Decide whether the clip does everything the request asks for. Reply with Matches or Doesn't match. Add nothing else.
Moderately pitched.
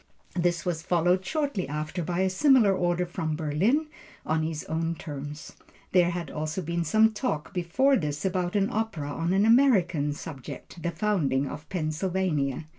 Matches